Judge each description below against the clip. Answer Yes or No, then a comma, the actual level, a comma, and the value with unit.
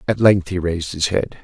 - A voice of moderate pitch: No, very low, 90 Hz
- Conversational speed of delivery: No, fast, 250 wpm